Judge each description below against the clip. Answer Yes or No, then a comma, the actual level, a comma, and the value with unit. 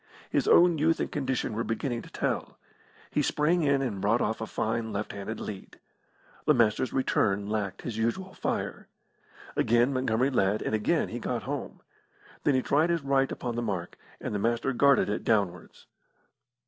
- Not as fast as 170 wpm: No, average, 175 wpm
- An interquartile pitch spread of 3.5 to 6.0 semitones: Yes, average, 4.4 semitones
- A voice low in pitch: Yes, low, 120 Hz